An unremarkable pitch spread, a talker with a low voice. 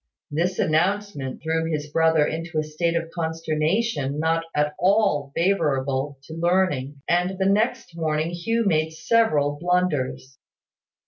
No: average, 3.5 semitones; medium, 160 Hz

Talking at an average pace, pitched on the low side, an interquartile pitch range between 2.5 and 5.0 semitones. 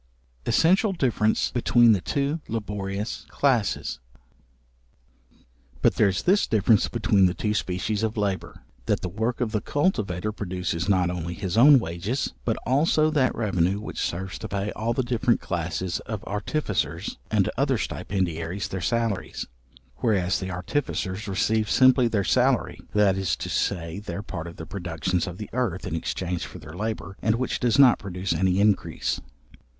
Yes: average, 160 wpm; low, 100 Hz; average, 4.2 semitones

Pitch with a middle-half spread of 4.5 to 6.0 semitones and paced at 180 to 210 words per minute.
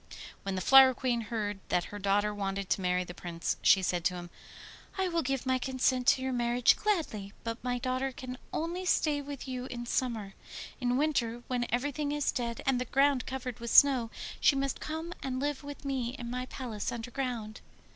No: average, 3.4 semitones; average, 195 wpm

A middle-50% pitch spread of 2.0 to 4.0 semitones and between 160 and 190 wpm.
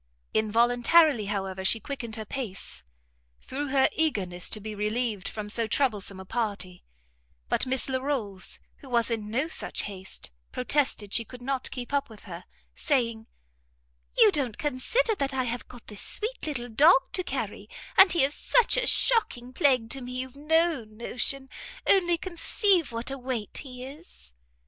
No: average, 4.9 semitones; average, 165 wpm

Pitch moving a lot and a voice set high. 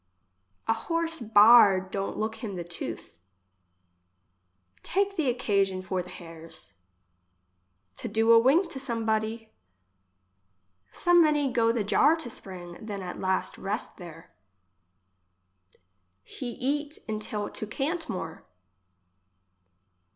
Yes: wide, 6.0 semitones; high, 220 Hz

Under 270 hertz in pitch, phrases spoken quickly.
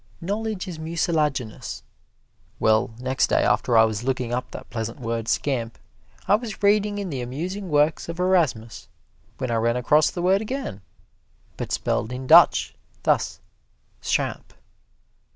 No: medium, 140 Hz; average, 145 wpm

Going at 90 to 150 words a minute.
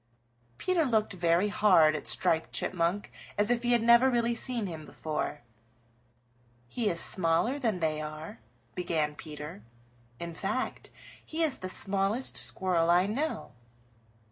Yes: average, 140 wpm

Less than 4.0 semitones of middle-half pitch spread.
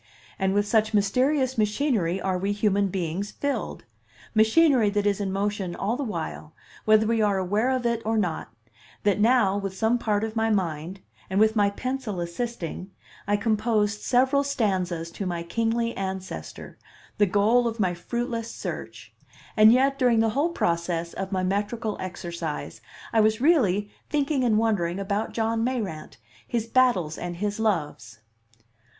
Yes: average, 3.5 semitones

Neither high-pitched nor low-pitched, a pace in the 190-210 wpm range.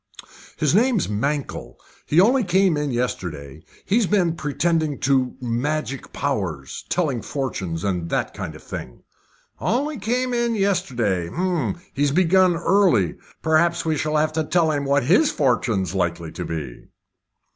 No: medium, 150 Hz; average, 140 wpm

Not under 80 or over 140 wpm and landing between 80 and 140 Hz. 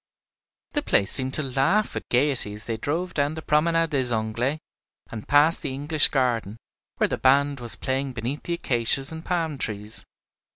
No: average, 175 wpm; low, 135 Hz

